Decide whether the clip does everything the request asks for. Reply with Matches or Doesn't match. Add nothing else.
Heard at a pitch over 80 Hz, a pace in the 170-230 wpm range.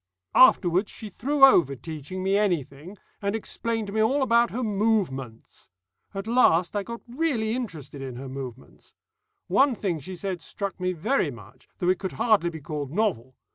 Matches